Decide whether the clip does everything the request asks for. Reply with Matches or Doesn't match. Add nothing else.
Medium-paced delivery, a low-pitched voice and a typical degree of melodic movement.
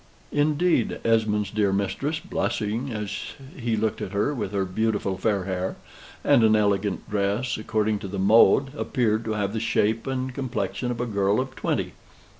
Matches